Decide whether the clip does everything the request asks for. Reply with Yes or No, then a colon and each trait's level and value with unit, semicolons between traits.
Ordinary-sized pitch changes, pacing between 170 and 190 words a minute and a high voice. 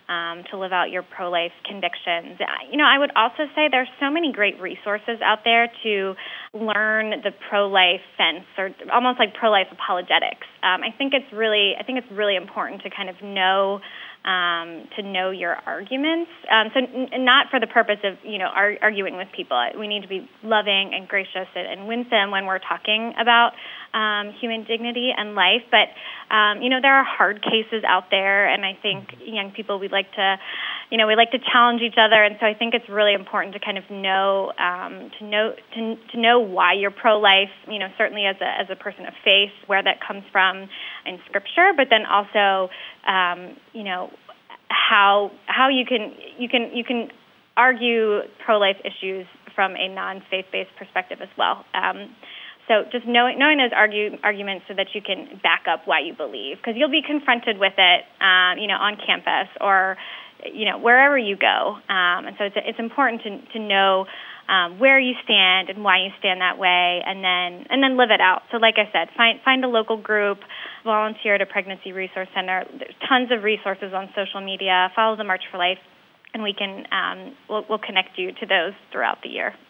No: average, 3.4 semitones; fast, 205 wpm; high, 210 Hz